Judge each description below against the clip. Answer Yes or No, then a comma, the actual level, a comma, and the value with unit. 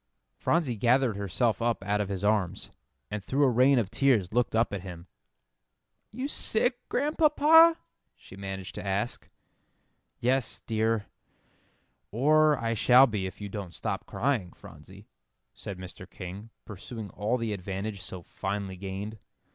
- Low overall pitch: Yes, low, 110 Hz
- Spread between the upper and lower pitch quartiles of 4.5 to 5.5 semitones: Yes, average, 4.8 semitones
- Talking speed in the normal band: Yes, average, 145 wpm